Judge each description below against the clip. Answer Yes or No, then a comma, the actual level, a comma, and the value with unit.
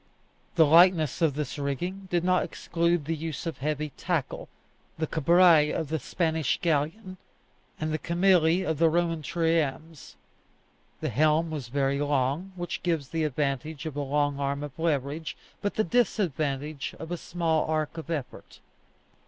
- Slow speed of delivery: No, average, 155 wpm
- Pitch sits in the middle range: Yes, medium, 160 Hz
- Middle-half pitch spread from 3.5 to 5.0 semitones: No, average, 2.7 semitones